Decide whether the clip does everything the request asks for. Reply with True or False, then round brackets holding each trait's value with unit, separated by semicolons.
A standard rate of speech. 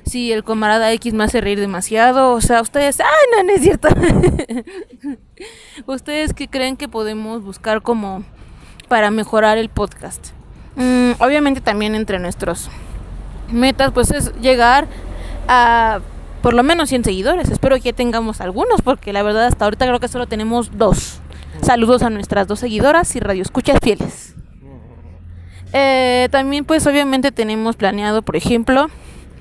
True (155 wpm)